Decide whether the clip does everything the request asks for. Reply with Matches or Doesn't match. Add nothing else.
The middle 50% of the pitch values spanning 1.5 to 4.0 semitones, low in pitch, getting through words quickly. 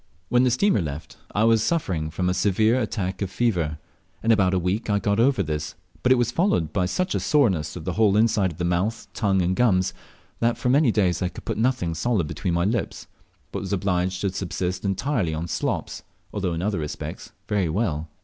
Doesn't match